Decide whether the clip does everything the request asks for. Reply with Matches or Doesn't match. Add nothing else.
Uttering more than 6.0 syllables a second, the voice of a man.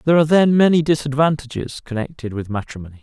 Matches